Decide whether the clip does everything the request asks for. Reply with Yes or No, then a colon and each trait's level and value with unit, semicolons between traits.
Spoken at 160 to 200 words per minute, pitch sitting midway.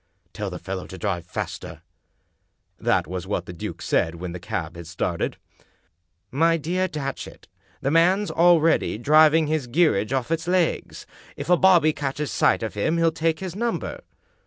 Yes: average, 175 wpm; medium, 150 Hz